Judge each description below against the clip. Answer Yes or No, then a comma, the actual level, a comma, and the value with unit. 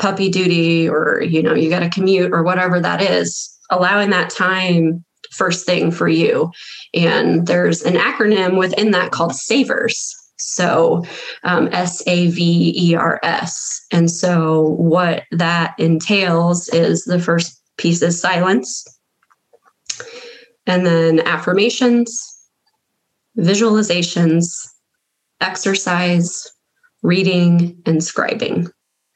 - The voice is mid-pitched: Yes, medium, 180 Hz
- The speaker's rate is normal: No, slow, 110 wpm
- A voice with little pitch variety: Yes, narrow, 2.2 semitones